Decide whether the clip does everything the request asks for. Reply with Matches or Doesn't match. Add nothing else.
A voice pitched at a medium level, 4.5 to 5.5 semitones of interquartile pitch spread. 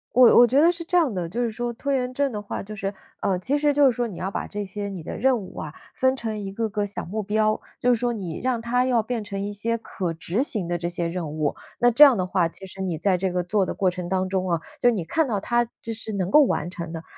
Doesn't match